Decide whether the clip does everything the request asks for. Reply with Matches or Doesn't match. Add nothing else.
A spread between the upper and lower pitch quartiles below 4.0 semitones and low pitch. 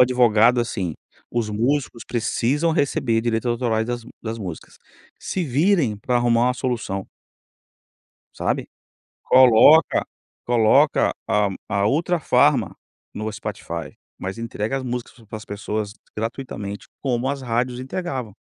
Matches